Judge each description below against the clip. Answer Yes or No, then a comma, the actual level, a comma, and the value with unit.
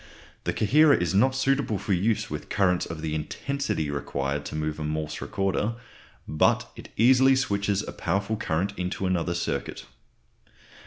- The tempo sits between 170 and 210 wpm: No, average, 155 wpm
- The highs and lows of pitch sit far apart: Yes, wide, 6.7 semitones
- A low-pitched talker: Yes, very low, 95 Hz